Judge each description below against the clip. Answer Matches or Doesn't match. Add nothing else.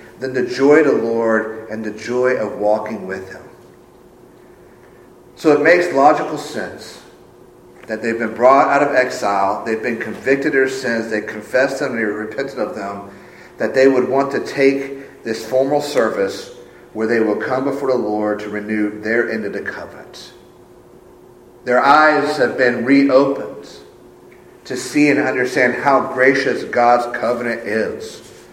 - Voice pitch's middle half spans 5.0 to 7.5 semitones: Doesn't match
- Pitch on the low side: Matches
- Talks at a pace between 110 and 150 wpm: Doesn't match